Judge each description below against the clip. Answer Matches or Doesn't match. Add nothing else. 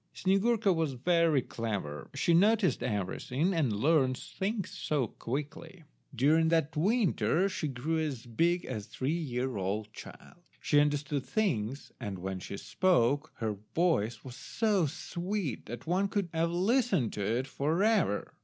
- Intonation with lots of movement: Matches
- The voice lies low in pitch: Doesn't match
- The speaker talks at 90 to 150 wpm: Matches